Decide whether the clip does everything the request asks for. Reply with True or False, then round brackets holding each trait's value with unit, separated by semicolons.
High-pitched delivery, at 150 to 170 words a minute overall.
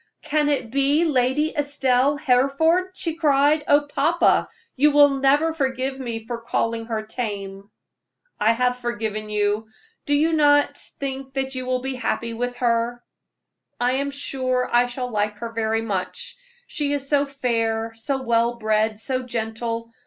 True (255 Hz; 155 wpm)